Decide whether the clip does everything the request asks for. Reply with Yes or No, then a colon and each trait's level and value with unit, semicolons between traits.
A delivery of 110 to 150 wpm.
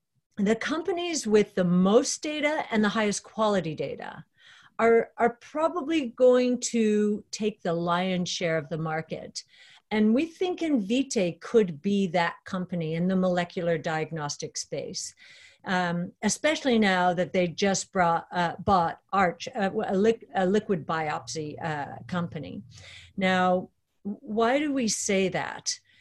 Yes: slow, 135 wpm